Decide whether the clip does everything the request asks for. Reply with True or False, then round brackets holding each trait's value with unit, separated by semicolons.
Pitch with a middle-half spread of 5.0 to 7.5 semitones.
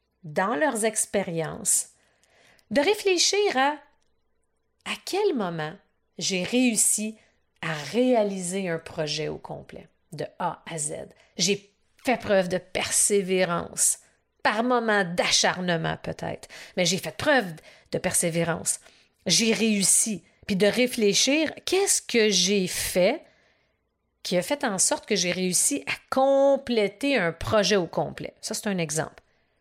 True (5.6 semitones)